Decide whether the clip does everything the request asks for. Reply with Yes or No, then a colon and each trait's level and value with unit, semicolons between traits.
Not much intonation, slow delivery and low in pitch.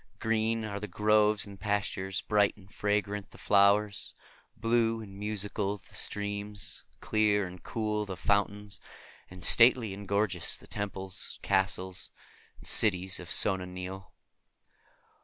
Yes: narrow, 1.8 semitones; slow, 130 wpm; low, 100 Hz